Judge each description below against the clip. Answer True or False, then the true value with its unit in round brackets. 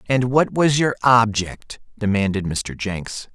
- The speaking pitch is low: True (110 Hz)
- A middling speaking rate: True (145 wpm)